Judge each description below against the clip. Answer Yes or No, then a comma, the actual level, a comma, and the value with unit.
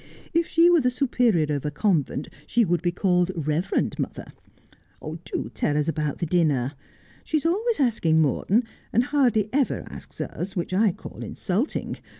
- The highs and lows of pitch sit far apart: Yes, wide, 7.9 semitones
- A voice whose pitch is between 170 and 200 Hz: Yes, medium, 185 Hz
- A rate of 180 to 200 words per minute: No, average, 165 wpm